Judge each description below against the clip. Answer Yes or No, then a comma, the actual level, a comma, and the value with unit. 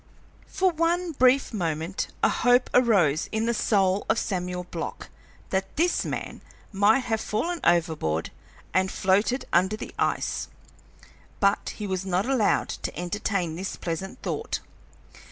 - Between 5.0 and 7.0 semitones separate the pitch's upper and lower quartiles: Yes, average, 5.3 semitones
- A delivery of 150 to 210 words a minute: No, slow, 135 wpm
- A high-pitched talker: Yes, high, 200 Hz